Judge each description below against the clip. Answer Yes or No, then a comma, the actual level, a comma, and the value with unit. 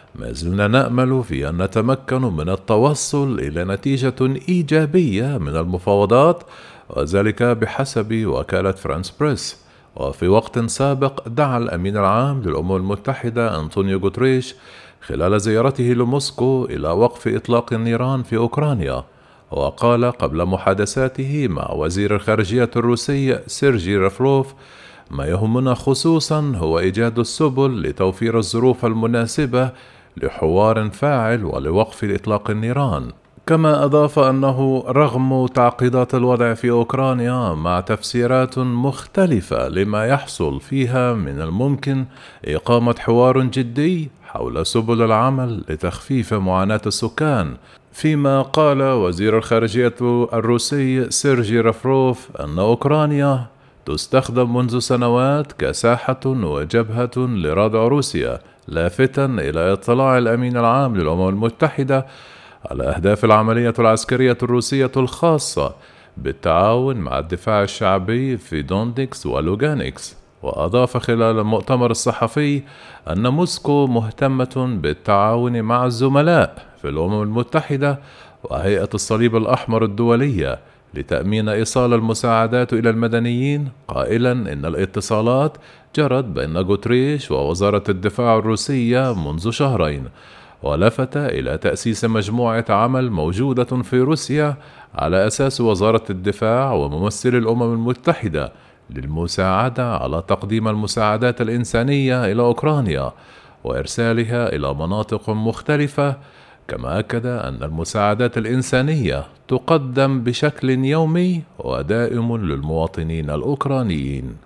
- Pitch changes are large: No, average, 4.0 semitones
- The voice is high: No, low, 120 Hz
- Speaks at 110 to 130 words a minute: No, average, 100 wpm